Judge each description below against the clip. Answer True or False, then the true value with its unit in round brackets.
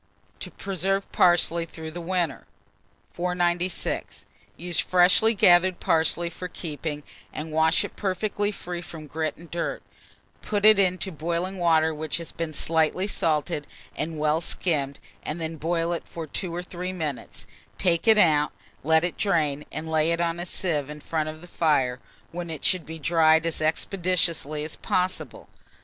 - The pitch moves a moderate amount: False (2.3 semitones)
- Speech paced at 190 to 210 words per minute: False (165 wpm)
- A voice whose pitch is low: False (165 Hz)